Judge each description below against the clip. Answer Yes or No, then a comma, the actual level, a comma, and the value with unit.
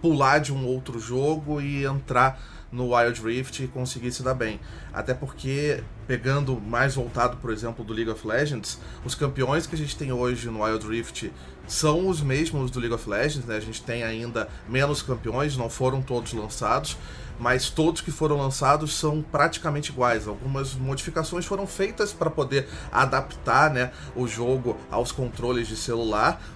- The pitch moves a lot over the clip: No, average, 3.7 semitones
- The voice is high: No, low, 130 Hz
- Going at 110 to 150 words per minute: No, average, 170 wpm